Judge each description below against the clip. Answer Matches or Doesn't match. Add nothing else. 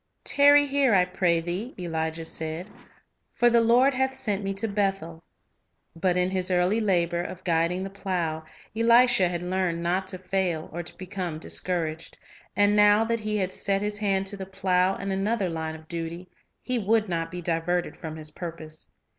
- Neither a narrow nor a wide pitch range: Matches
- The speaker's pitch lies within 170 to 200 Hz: Matches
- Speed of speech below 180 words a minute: Doesn't match